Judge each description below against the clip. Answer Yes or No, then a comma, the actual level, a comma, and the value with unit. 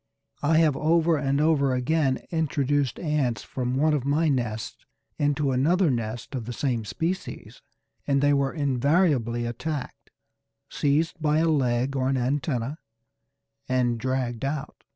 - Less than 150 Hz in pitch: Yes, medium, 140 Hz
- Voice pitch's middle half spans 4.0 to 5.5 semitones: No, average, 3.4 semitones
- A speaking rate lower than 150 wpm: Yes, average, 140 wpm